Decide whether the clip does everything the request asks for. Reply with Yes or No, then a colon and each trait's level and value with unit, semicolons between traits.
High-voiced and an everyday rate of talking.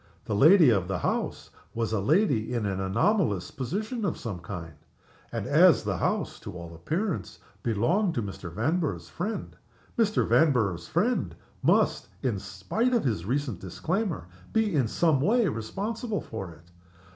No: low, 125 Hz; average, 155 wpm